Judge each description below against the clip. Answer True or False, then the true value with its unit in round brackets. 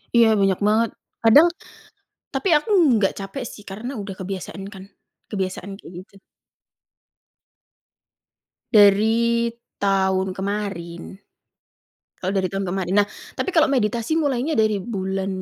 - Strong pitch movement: False (3.3 semitones)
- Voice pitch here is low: False (205 Hz)